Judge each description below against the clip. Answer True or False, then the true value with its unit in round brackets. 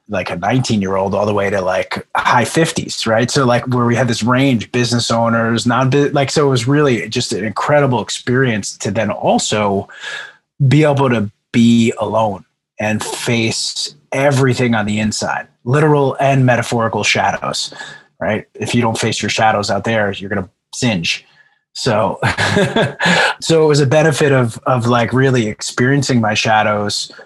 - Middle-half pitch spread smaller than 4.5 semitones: True (3.8 semitones)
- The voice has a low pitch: True (120 Hz)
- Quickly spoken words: False (155 wpm)